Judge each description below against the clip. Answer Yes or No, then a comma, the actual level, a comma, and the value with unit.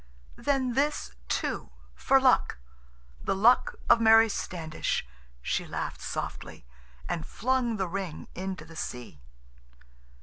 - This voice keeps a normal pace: No, slow, 110 wpm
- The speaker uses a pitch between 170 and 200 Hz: Yes, high, 190 Hz